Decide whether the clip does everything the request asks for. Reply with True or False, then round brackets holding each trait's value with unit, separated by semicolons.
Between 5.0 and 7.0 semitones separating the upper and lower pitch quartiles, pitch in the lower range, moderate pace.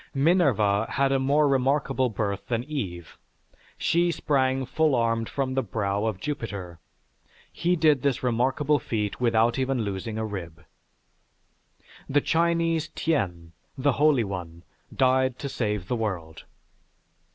False (5.4 semitones; 125 Hz; 130 wpm)